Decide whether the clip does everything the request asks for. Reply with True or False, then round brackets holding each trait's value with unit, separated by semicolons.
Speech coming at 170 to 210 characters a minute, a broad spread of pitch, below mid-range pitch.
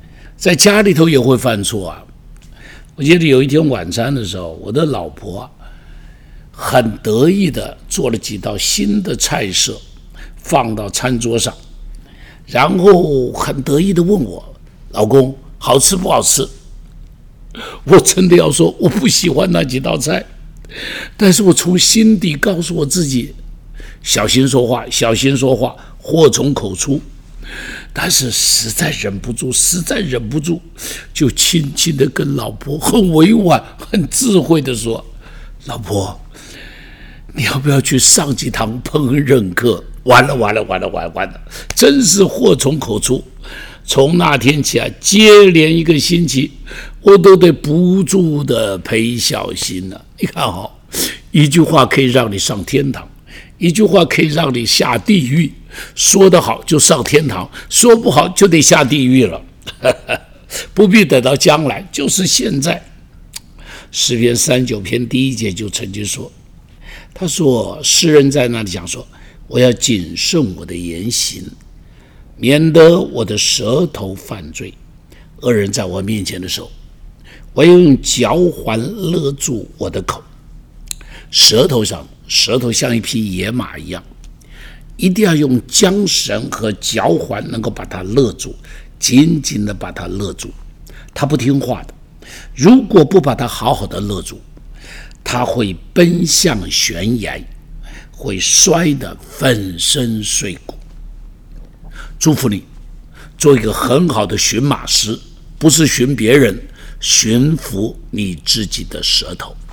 True (200 characters per minute; 6.8 semitones; 130 Hz)